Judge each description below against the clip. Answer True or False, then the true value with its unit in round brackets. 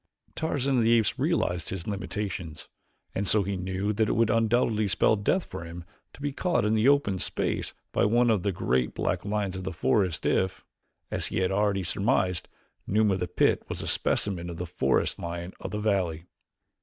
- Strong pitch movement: False (3.4 semitones)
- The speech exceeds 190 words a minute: True (200 wpm)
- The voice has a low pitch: True (100 Hz)